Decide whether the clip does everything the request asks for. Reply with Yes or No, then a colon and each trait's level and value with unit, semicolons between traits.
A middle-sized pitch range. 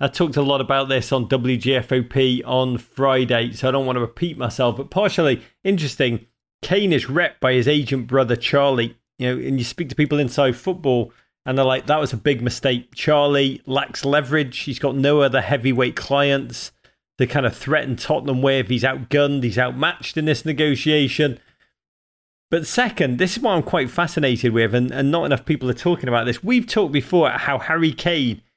Yes: average, 3.2 semitones